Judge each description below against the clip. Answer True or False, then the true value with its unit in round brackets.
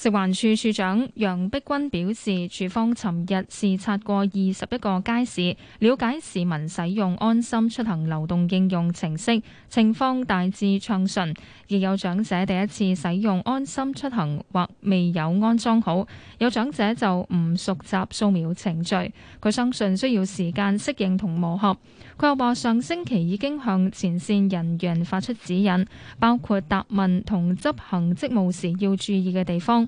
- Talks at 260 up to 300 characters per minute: False (240 characters per minute)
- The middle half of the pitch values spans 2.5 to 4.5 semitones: True (3.8 semitones)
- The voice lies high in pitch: True (195 Hz)